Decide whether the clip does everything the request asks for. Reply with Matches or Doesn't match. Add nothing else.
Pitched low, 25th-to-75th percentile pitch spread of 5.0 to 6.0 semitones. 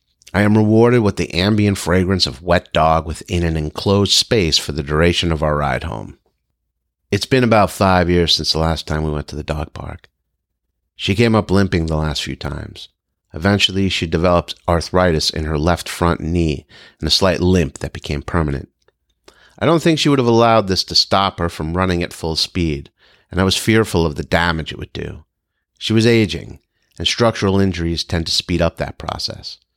Doesn't match